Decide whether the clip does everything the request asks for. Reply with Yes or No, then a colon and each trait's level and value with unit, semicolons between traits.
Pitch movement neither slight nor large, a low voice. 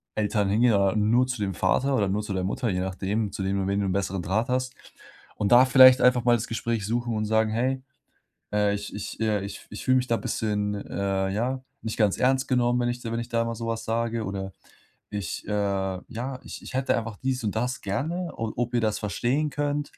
Yes: average, 3.5 semitones; low, 110 Hz